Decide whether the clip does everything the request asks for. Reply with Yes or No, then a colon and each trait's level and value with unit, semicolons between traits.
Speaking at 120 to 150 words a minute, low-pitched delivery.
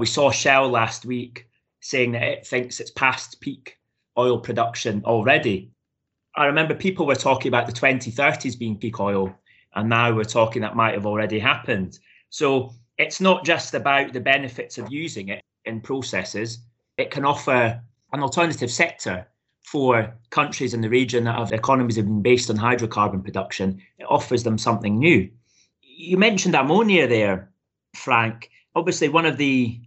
No: average, 165 wpm; low, 120 Hz